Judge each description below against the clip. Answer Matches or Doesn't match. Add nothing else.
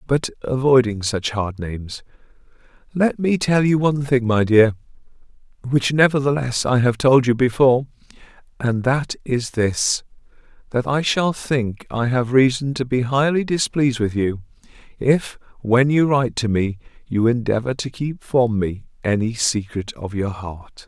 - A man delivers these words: Matches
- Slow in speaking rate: Doesn't match